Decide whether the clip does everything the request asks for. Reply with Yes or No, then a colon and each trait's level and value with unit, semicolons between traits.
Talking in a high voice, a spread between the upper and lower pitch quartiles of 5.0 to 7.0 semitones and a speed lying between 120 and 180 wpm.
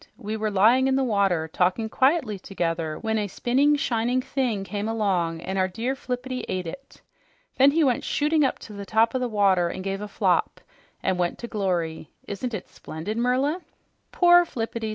No: high, 220 Hz; average, 5.3 semitones; average, 190 wpm